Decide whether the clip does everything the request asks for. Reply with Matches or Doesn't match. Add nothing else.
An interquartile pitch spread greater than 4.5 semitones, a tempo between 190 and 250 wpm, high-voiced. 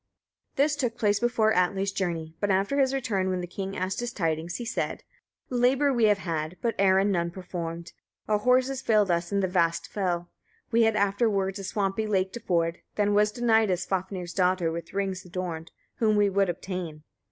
Doesn't match